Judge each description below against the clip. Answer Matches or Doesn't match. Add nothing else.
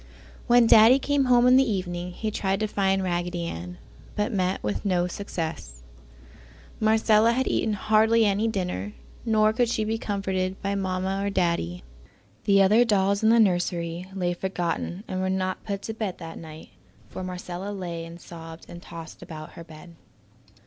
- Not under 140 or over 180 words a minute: Matches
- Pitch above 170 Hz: Matches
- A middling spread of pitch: Matches